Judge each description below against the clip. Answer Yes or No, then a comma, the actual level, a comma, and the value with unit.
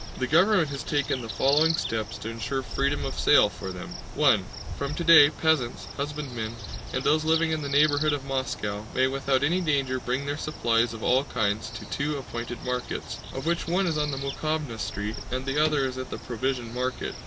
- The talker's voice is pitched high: No, low, 135 Hz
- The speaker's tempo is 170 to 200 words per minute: Yes, average, 195 wpm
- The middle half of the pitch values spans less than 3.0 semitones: No, average, 3.7 semitones